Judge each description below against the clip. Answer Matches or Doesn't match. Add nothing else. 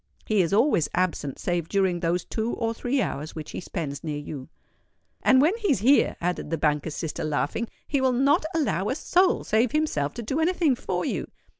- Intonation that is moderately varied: Doesn't match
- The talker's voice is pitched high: Matches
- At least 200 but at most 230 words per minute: Matches